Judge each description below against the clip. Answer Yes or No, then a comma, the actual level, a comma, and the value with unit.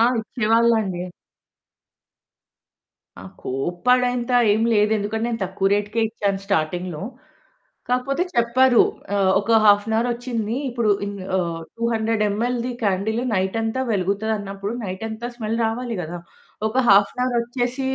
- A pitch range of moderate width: Yes, average, 3.1 semitones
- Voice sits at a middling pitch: No, high, 220 Hz